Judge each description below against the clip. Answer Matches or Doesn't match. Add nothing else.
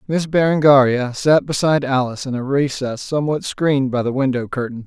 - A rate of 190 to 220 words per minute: Doesn't match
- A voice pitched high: Doesn't match